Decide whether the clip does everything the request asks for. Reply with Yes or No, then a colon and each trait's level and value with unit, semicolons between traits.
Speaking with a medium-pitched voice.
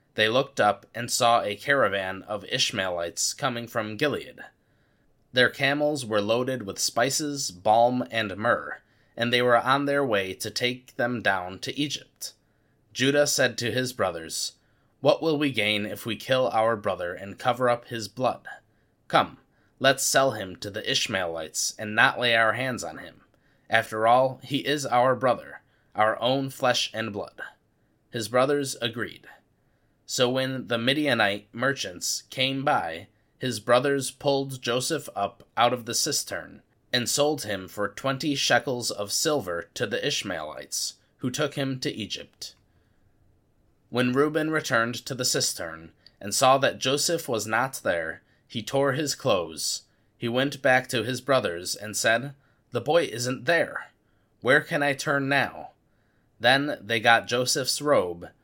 No: low, 125 Hz